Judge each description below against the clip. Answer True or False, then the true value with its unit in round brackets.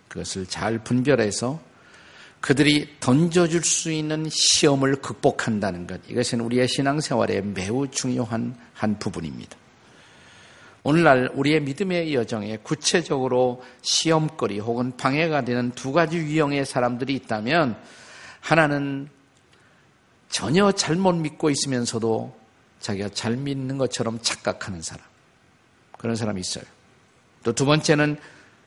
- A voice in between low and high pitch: False (130 Hz)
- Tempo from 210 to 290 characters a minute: True (275 characters per minute)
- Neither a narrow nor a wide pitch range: True (4.6 semitones)